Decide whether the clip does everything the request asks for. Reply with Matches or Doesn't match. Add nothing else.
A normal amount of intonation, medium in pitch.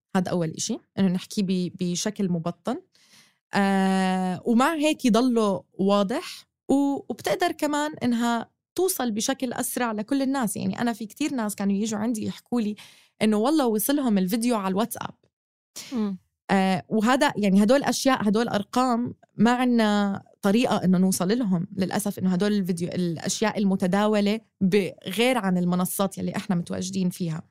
Doesn't match